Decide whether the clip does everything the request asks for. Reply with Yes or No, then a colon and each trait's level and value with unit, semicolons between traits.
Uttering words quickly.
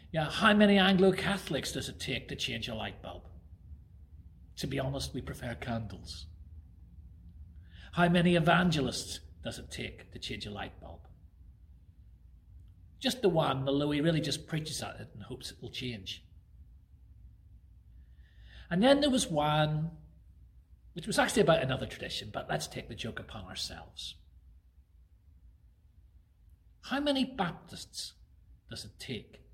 No: average, 140 wpm